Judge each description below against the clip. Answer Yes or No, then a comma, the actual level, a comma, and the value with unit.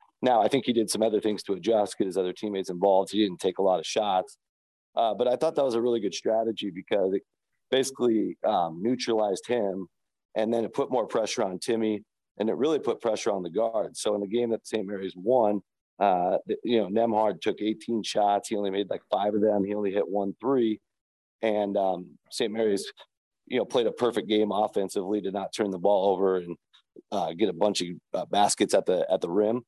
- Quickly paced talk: Yes, fast, 225 wpm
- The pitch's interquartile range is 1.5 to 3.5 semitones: Yes, narrow, 2.6 semitones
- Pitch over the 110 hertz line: No, low, 105 Hz